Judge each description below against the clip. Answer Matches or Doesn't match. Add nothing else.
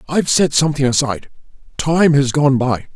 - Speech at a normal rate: Matches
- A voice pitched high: Doesn't match